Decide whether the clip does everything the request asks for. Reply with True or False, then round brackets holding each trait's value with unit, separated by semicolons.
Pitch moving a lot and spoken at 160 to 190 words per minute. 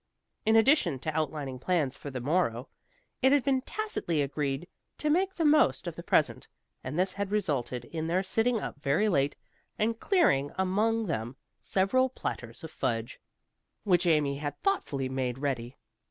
True (8.5 semitones; 165 wpm)